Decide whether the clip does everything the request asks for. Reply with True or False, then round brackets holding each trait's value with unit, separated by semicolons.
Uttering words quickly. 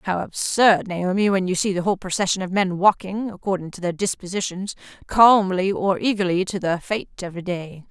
False (165 wpm)